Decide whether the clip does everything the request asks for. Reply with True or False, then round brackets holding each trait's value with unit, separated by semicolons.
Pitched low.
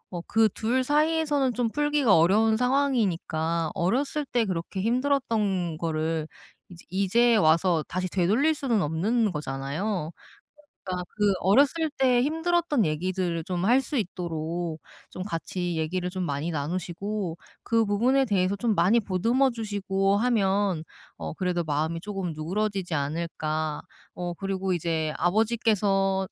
False (195 Hz)